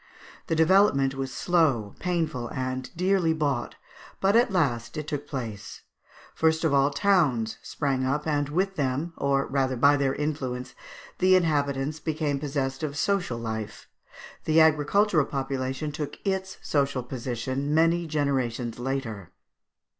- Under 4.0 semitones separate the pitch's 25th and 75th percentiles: Yes, average, 3.6 semitones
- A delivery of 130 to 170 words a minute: Yes, slow, 135 wpm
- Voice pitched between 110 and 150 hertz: Yes, medium, 140 Hz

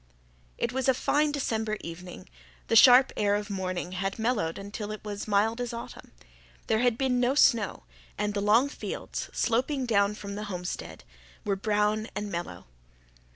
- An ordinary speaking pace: Yes, average, 170 wpm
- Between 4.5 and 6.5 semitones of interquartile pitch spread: No, average, 3.4 semitones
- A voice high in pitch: Yes, high, 215 Hz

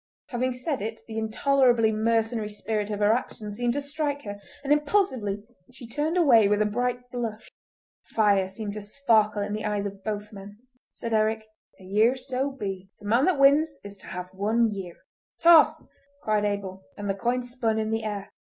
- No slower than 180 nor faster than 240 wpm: Yes, average, 190 wpm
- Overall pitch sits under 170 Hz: No, high, 220 Hz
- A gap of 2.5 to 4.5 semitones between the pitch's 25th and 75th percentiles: Yes, average, 3.4 semitones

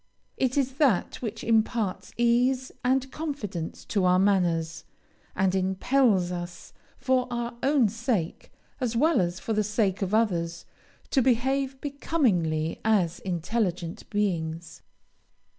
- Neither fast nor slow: No, slow, 125 wpm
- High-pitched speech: Yes, high, 215 Hz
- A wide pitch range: Yes, wide, 6.2 semitones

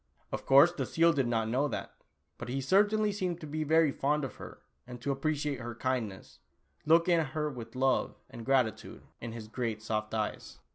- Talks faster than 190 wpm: Yes, average, 200 wpm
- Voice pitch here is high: No, low, 135 Hz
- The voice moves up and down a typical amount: Yes, average, 5.0 semitones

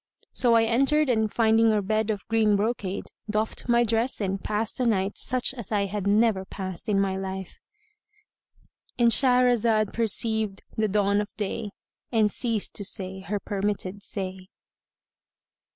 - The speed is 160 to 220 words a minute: No, average, 150 wpm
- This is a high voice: Yes, high, 215 Hz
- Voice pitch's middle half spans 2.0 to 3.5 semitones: Yes, average, 2.8 semitones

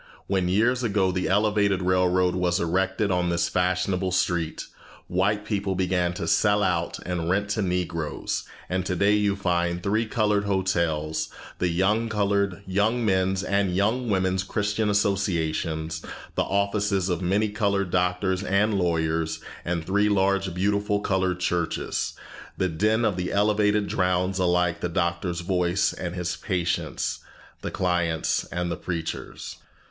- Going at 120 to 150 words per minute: Yes, average, 140 wpm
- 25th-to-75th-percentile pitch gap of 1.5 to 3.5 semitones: Yes, narrow, 2.4 semitones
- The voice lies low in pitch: Yes, very low, 95 Hz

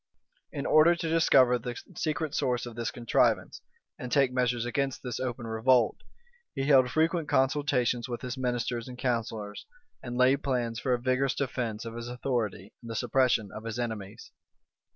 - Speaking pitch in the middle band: No, low, 125 Hz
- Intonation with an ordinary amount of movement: No, narrow, 2.3 semitones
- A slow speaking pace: No, average, 175 wpm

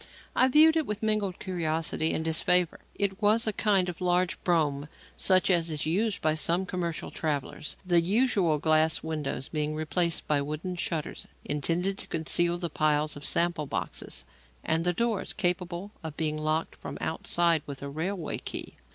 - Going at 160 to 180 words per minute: Yes, average, 170 wpm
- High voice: No, medium, 170 Hz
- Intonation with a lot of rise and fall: No, average, 3.1 semitones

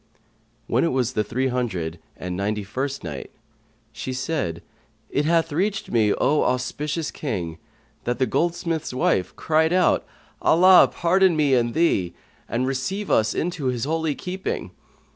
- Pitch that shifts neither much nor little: No, wide, 6.3 semitones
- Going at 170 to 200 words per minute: No, average, 145 wpm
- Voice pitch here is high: No, low, 130 Hz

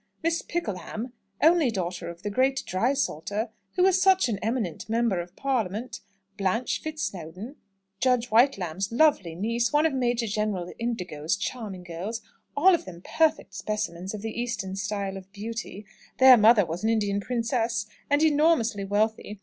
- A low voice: No, high, 220 Hz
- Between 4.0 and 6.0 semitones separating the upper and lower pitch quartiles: Yes, average, 4.6 semitones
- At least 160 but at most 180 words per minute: No, average, 150 wpm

